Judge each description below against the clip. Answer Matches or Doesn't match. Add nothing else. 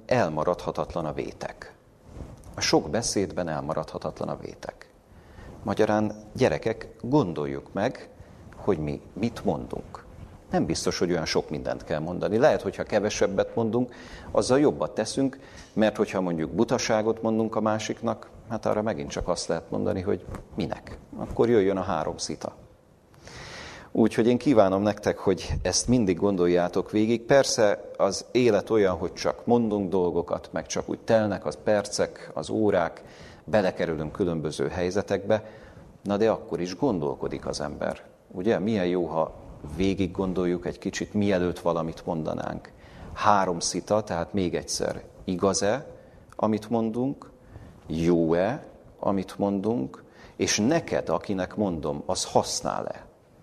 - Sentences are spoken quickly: Doesn't match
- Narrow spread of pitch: Doesn't match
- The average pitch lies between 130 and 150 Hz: Doesn't match